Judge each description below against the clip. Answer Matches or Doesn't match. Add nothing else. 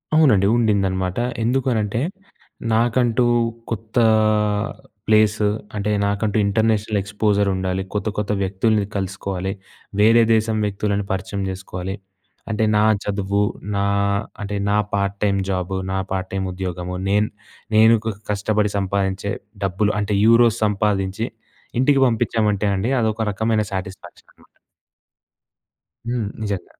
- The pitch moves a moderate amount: Doesn't match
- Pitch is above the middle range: Doesn't match